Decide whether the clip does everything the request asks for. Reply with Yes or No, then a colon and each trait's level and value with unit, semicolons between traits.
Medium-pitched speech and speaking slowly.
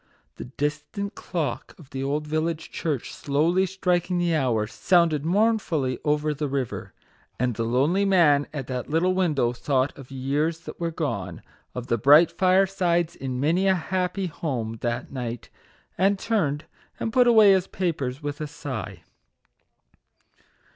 No: medium, 155 Hz; average, 150 wpm